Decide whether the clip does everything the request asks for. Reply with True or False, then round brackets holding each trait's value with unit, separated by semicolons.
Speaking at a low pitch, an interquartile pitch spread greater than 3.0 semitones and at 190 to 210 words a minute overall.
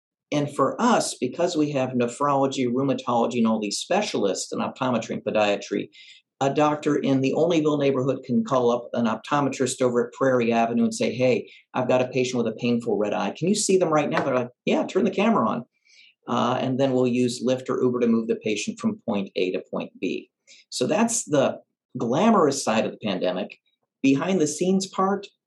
True (130 Hz; 4.0 semitones; 205 wpm)